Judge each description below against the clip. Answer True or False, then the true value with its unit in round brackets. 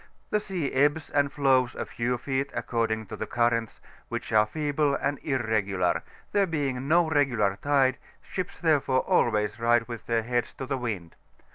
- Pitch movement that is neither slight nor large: True (3.9 semitones)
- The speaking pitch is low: True (130 Hz)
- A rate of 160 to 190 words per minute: True (165 wpm)